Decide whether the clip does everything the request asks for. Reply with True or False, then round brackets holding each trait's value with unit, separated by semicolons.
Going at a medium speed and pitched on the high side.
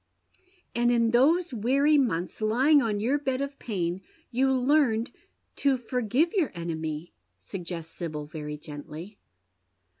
False (130 wpm; 235 Hz)